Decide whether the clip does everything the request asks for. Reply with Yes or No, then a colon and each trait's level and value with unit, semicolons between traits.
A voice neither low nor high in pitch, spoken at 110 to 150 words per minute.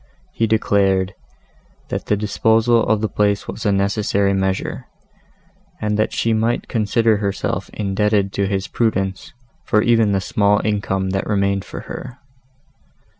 No: low, 105 Hz; average, 140 wpm